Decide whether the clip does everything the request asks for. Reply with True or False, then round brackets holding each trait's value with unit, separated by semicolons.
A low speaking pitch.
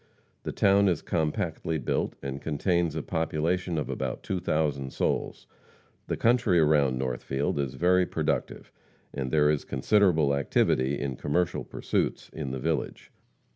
True (75 Hz)